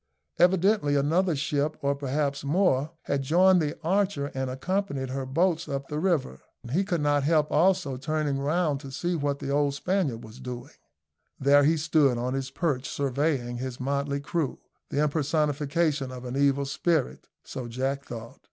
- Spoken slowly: No, average, 165 wpm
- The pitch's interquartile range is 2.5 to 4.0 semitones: Yes, average, 3.0 semitones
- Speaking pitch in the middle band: Yes, medium, 145 Hz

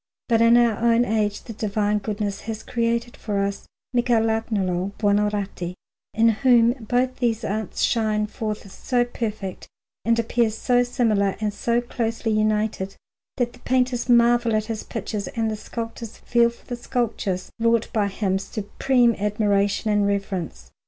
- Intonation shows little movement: Yes, narrow, 2.3 semitones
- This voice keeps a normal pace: Yes, average, 150 wpm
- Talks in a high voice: Yes, high, 220 Hz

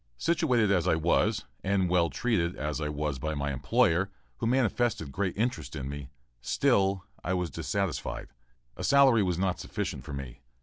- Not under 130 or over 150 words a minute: No, average, 170 wpm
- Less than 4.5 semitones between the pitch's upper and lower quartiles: No, wide, 5.5 semitones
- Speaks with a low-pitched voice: Yes, very low, 90 Hz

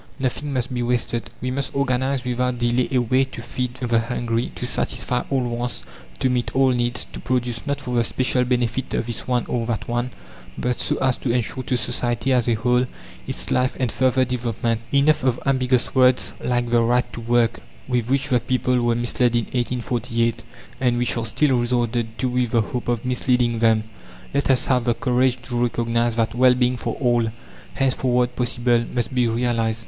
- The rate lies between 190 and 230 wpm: Yes, average, 195 wpm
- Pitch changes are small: Yes, narrow, 1.2 semitones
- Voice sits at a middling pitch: No, low, 125 Hz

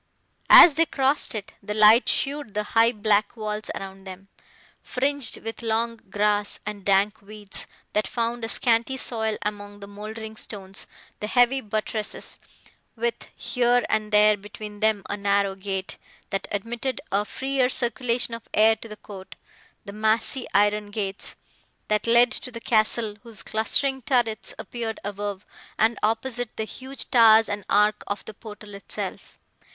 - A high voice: Yes, high, 215 Hz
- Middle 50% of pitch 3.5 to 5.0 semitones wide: No, narrow, 2.4 semitones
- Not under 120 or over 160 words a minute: Yes, average, 155 wpm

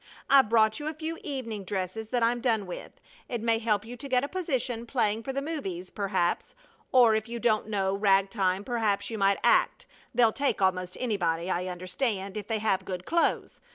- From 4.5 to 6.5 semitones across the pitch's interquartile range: No, average, 4.1 semitones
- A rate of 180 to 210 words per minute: Yes, average, 200 wpm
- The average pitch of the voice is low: No, high, 220 Hz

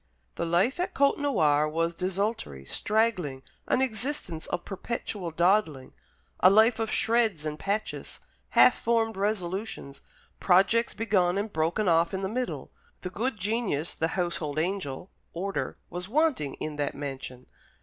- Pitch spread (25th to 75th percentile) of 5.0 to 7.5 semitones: Yes, wide, 5.5 semitones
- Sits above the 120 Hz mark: Yes, high, 190 Hz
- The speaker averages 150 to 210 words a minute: No, average, 140 wpm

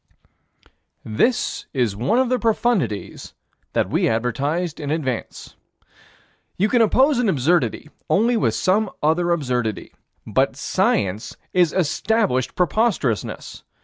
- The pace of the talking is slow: Yes, slow, 115 wpm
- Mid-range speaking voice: Yes, medium, 170 Hz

